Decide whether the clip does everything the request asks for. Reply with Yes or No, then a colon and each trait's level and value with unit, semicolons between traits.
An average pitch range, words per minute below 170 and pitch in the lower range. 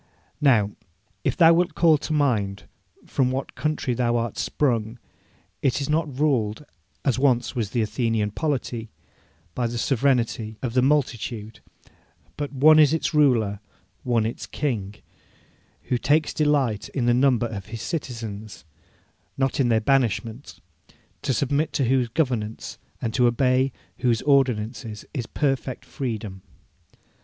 Yes: average, 3.9 semitones; average, 140 wpm; low, 125 Hz